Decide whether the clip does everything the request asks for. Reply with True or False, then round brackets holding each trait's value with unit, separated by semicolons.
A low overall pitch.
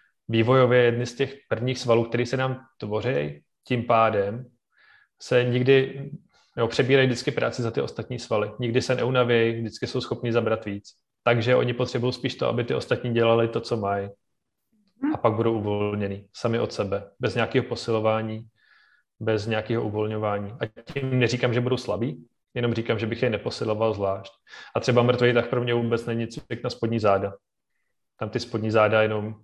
True (115 Hz)